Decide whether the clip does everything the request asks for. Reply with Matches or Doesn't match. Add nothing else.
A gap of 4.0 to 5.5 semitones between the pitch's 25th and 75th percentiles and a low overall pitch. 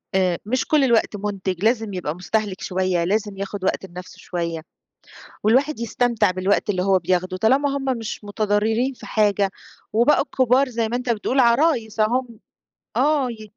Doesn't match